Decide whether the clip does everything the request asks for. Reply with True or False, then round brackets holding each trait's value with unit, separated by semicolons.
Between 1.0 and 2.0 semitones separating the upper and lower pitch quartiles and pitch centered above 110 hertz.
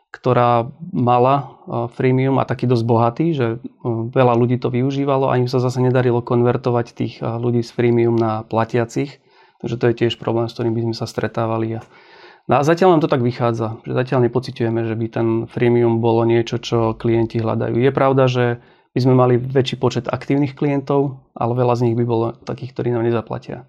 True (1.7 semitones; 120 Hz)